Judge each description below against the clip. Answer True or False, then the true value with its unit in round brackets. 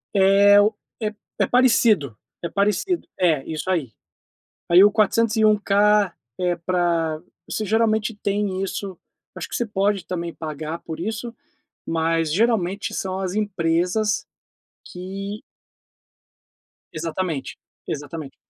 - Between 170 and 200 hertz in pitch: True (190 Hz)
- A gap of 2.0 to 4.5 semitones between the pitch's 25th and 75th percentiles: True (4.0 semitones)